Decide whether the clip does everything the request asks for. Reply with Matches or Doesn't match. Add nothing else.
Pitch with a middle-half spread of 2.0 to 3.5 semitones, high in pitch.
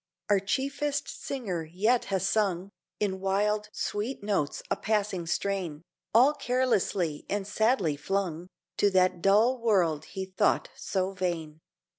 Matches